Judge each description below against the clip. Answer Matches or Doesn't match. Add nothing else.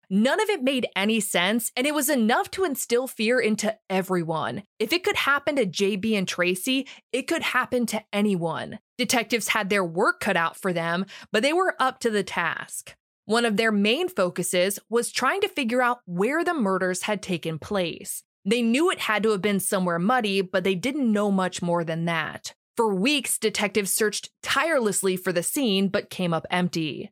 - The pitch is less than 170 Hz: Doesn't match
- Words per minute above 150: Matches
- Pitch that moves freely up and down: Doesn't match